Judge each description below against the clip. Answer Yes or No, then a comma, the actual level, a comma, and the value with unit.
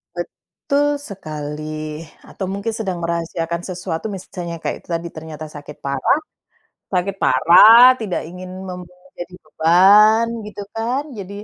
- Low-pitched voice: No, medium, 180 Hz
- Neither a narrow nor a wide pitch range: Yes, average, 3.8 semitones